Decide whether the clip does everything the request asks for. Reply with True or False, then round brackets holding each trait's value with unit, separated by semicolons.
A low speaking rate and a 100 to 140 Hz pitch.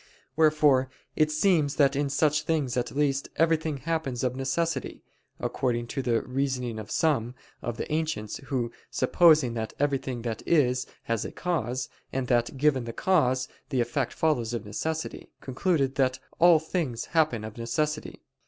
False (155 wpm; 135 Hz)